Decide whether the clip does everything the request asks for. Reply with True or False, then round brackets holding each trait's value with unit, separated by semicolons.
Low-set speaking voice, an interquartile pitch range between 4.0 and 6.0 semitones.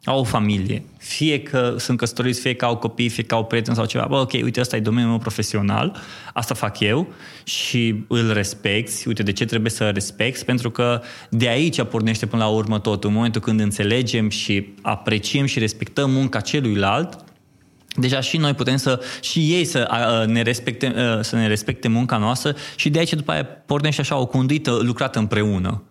False (120 Hz; 3.3 semitones)